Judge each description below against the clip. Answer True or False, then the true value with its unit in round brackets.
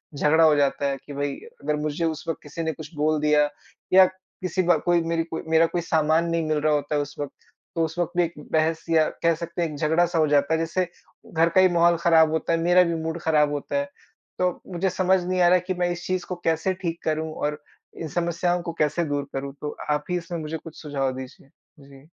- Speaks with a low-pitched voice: False (160 Hz)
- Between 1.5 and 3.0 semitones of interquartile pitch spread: True (2.4 semitones)